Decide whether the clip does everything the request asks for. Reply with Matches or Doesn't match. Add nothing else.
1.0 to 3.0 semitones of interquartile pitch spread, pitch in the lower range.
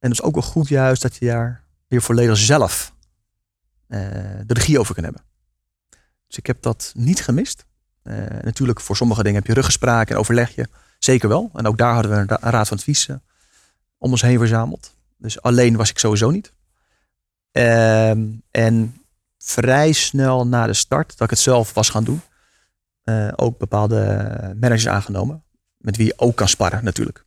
Matches